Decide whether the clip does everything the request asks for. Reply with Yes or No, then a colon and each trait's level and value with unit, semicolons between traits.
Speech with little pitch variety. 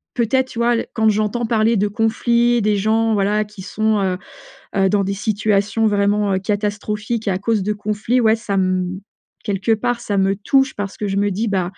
Yes: narrow, 2.1 semitones